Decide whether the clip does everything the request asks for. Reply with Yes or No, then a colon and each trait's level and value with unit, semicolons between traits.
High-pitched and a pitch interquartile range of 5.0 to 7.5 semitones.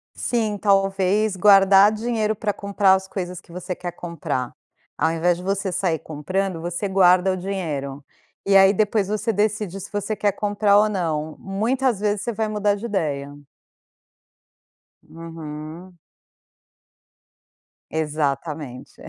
No: high, 195 Hz; average, 3.7 semitones